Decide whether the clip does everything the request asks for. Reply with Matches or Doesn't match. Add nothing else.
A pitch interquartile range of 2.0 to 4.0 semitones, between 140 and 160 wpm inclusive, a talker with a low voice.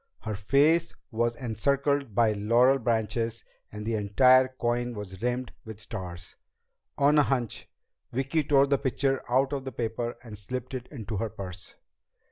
Matches